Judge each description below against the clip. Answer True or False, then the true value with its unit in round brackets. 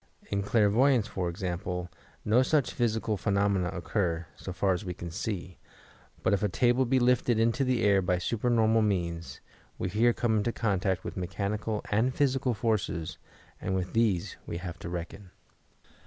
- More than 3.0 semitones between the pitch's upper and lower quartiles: True (4.2 semitones)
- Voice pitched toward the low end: True (100 Hz)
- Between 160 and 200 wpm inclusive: True (165 wpm)